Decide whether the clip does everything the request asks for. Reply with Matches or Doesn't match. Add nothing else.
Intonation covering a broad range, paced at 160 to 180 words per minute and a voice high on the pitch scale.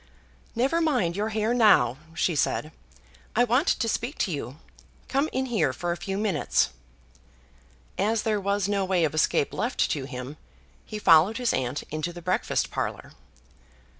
Matches